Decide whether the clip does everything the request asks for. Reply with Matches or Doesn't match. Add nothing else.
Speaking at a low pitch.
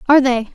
Doesn't match